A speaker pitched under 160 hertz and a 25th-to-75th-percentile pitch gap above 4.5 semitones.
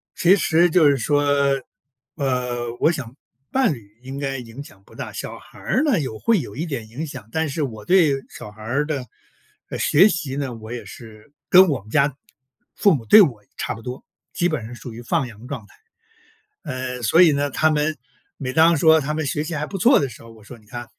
Yes: medium, 140 Hz; average, 4.9 semitones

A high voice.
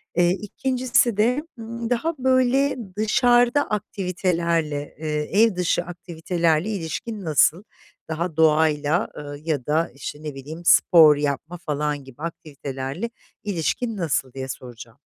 No: medium, 170 Hz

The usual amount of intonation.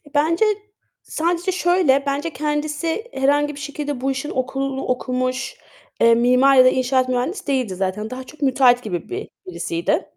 Yes: average, 3.0 semitones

